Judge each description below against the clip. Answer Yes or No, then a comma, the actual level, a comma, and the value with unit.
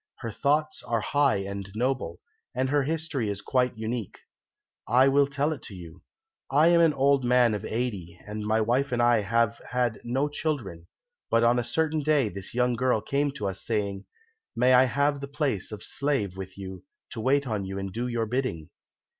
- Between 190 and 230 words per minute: Yes, average, 195 wpm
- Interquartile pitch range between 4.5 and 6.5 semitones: Yes, average, 4.9 semitones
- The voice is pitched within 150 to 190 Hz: No, low, 120 Hz